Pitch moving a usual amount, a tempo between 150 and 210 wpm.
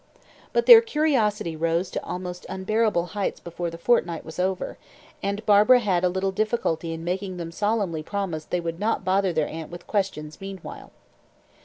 Yes: average, 3.7 semitones; average, 175 wpm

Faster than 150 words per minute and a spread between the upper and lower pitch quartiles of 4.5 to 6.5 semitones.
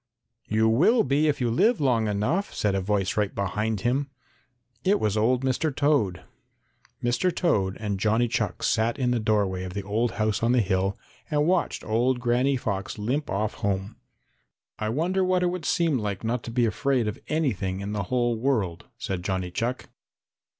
Yes: average, 185 wpm; average, 5.0 semitones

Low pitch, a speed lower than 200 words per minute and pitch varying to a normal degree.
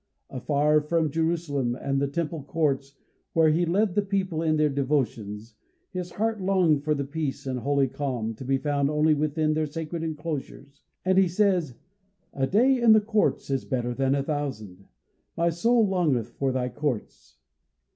No: medium, 150 Hz; average, 170 wpm; average, 3.8 semitones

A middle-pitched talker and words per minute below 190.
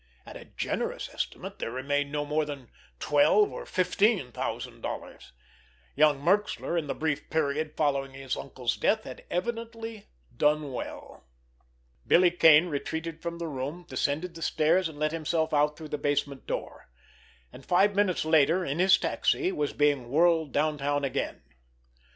Yes: medium, 155 Hz; average, 150 wpm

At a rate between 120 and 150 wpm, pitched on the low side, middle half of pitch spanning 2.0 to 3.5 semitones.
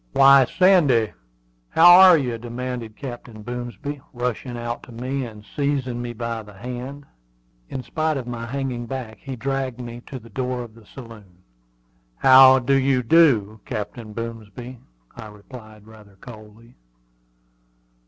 Yes: average, 140 wpm; low, 120 Hz; average, 2.8 semitones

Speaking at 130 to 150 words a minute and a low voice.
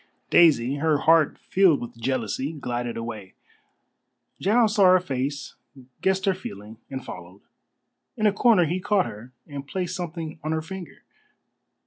No: average, 145 wpm; medium, 155 Hz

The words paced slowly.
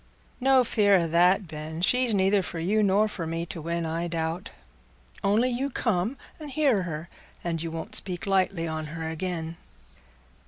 No: average, 170 wpm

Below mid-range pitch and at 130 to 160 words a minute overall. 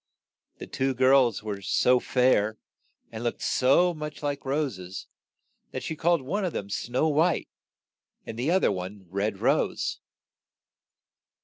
Yes: low, 130 Hz; average, 140 wpm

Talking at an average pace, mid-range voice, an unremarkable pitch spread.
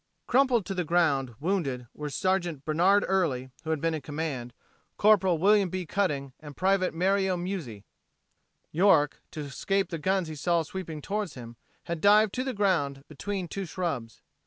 Yes: average, 165 wpm; medium, 175 Hz; average, 4.8 semitones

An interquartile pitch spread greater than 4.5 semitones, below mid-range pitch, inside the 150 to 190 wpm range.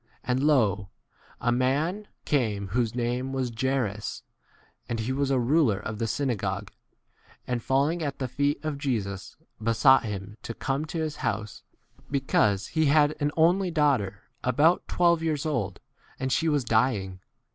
Yes: average, 5.2 semitones; low, 130 Hz; average, 160 wpm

